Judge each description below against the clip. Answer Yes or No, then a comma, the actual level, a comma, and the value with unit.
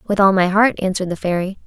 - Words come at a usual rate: No, fast, 250 wpm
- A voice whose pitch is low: No, high, 190 Hz